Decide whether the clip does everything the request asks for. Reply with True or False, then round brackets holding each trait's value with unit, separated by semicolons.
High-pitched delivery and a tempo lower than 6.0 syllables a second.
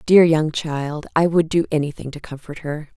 False (155 Hz; 4.8 syllables/s)